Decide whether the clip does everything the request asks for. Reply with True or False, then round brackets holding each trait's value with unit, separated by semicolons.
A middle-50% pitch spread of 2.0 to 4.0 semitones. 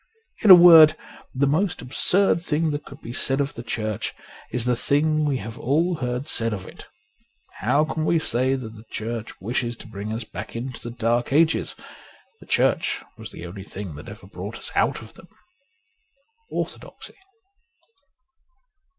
False (5.5 semitones)